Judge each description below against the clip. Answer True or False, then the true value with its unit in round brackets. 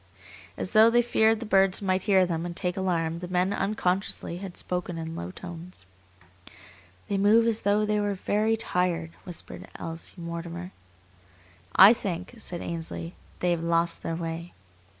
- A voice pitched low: False (180 Hz)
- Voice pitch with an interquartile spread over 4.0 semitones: False (3.2 semitones)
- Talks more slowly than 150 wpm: False (160 wpm)